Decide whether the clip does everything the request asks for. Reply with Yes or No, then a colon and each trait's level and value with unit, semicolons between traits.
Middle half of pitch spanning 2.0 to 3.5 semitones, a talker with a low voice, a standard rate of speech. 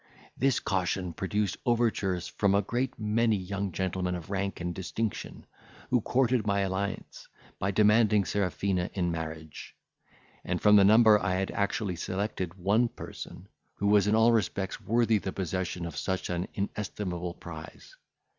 Yes: narrow, 2.6 semitones; low, 100 Hz; average, 150 wpm